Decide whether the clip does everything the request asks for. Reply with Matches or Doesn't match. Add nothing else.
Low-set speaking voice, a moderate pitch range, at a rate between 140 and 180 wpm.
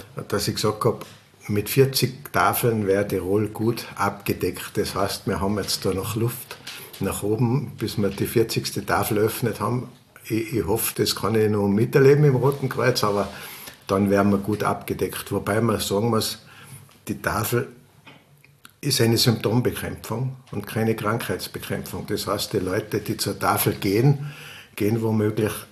Matches